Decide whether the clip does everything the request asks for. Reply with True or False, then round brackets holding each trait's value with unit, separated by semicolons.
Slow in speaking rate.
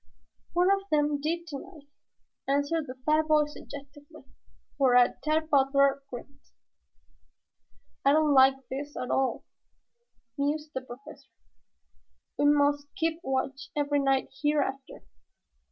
True (115 wpm)